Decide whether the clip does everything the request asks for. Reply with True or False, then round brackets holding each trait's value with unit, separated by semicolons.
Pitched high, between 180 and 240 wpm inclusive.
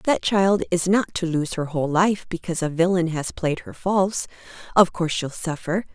False (175 Hz; 200 wpm)